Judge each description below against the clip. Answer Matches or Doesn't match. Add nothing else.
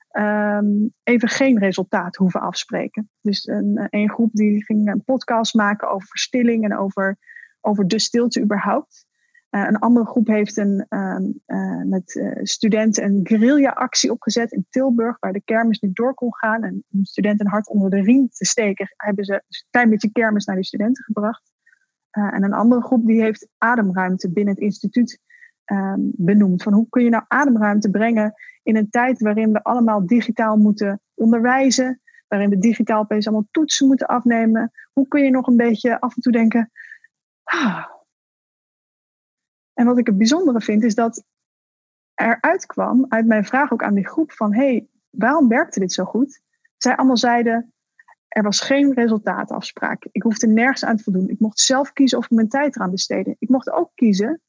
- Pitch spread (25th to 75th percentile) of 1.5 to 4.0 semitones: Matches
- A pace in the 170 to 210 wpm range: Matches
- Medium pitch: Doesn't match